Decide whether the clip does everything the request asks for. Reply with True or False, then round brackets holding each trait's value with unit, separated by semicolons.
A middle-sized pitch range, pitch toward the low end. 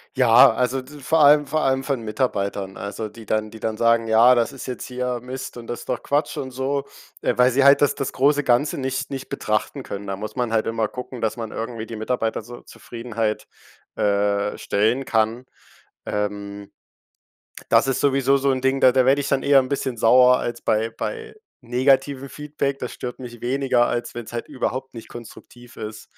True (3.1 semitones; 125 Hz)